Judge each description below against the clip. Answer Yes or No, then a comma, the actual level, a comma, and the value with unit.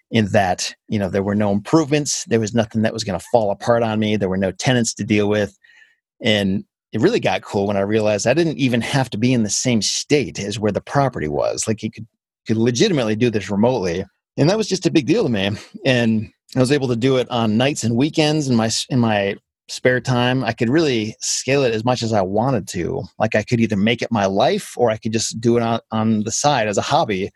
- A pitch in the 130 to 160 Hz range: No, low, 115 Hz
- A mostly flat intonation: No, average, 3.3 semitones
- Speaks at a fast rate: Yes, fast, 255 wpm